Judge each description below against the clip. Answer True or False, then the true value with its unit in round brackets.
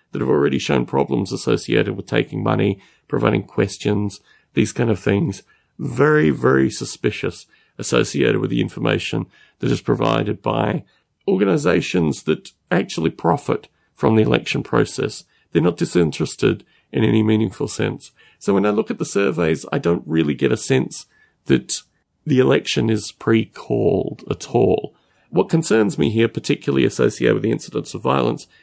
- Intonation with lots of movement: True (6.9 semitones)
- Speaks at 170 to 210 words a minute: False (150 wpm)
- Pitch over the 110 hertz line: False (100 Hz)